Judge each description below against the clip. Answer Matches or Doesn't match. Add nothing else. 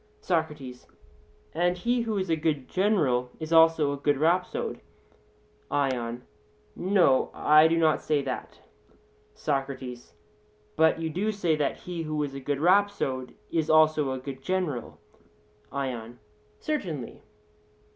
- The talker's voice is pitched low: Doesn't match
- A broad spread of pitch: Doesn't match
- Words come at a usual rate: Doesn't match